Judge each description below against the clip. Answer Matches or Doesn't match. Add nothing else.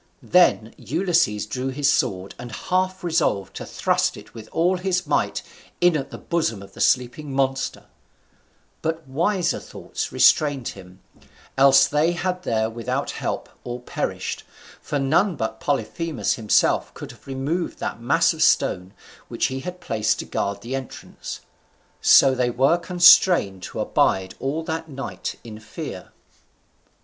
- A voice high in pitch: Doesn't match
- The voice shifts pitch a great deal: Matches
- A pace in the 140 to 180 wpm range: Matches